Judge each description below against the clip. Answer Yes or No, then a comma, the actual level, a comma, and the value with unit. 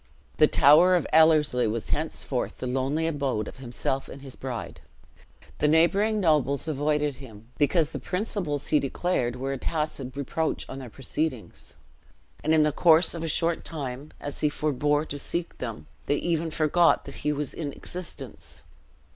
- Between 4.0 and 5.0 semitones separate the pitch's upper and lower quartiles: No, average, 3.2 semitones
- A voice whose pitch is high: No, medium, 150 Hz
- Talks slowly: No, average, 165 wpm